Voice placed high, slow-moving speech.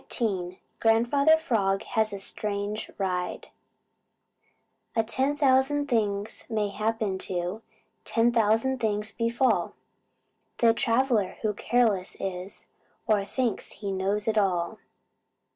Yes: high, 215 Hz; slow, 110 wpm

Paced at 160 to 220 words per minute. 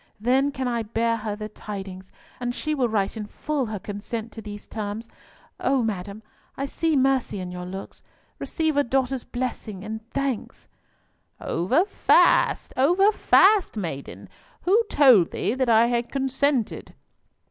No: average, 150 wpm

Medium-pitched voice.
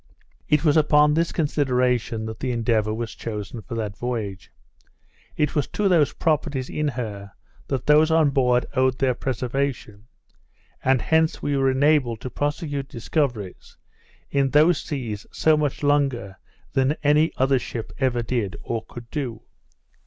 No: low, 130 Hz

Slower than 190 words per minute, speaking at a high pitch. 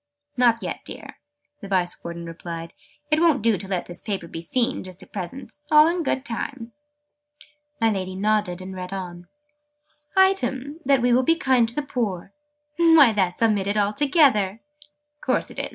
Yes: average, 170 wpm; high, 220 Hz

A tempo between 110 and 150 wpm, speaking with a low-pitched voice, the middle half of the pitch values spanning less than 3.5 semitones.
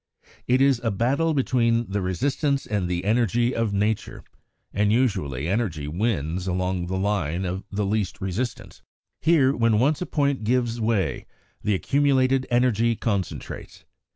No: average, 145 wpm; low, 110 Hz; average, 5.1 semitones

